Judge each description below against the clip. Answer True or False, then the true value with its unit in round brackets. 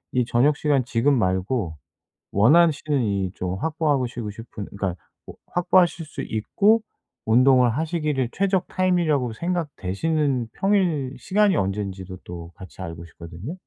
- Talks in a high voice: False (130 Hz)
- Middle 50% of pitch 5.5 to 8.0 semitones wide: False (8.4 semitones)